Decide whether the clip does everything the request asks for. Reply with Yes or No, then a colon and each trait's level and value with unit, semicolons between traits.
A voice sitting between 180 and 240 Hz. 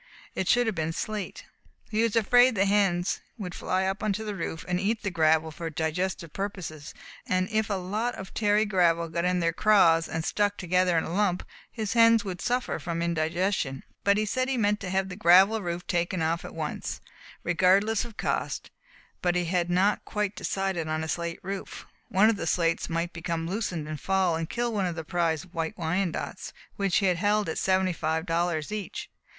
Yes: medium, 185 Hz